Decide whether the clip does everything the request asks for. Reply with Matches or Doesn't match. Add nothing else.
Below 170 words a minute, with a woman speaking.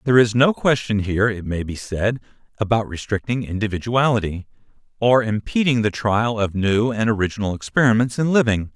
Doesn't match